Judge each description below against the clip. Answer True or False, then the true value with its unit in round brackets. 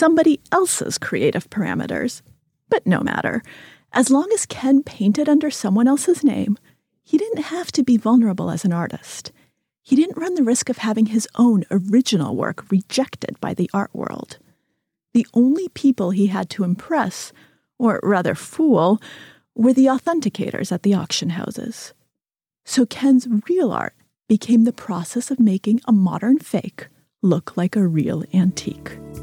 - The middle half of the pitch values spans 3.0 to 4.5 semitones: False (5.6 semitones)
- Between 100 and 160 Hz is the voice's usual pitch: False (235 Hz)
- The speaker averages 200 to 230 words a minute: False (155 wpm)